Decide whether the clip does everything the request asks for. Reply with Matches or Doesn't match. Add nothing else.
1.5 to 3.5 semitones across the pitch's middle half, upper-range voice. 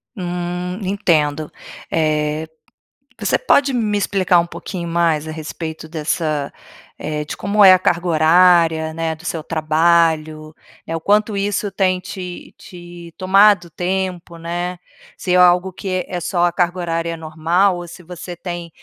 Doesn't match